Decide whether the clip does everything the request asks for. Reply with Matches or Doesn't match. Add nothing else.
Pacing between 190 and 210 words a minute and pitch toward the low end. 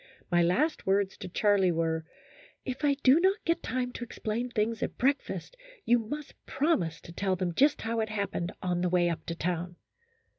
Doesn't match